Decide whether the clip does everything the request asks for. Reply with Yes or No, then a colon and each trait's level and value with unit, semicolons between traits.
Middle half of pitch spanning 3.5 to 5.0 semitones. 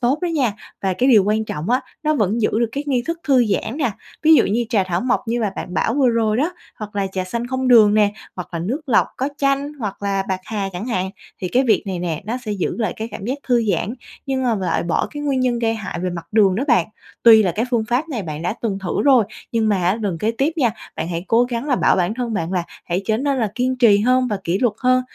Yes: average, 4.7 semitones